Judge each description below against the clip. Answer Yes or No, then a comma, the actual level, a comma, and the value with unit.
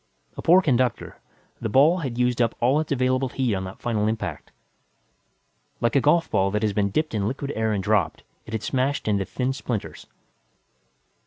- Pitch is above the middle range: No, low, 120 Hz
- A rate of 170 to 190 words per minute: Yes, average, 180 wpm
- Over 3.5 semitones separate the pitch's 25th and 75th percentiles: Yes, average, 4.1 semitones